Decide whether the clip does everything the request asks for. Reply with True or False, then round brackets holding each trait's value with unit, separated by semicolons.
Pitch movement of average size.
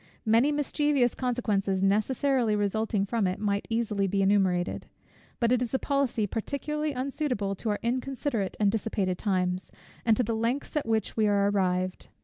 True (4.1 semitones)